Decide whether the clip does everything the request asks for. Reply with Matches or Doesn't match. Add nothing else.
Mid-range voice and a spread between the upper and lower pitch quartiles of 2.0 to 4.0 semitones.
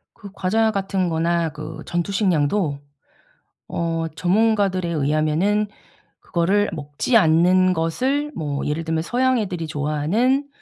Doesn't match